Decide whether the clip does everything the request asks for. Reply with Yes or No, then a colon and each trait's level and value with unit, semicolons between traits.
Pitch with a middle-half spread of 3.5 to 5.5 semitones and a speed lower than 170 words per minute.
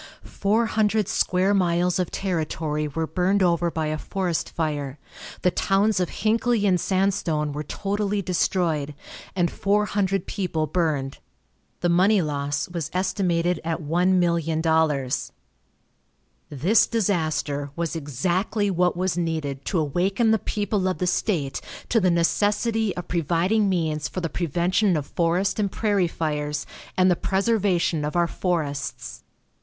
Yes: average, 3.8 semitones; average, 140 wpm